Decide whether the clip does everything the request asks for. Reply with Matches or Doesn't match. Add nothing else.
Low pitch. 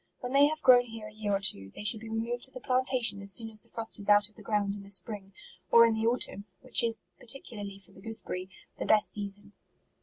Doesn't match